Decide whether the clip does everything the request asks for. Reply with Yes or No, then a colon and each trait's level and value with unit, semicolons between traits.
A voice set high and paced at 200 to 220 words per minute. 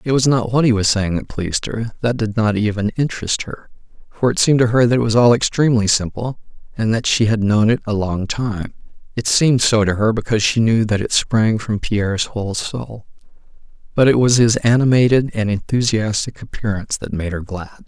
No: low, 110 Hz; fast, 205 wpm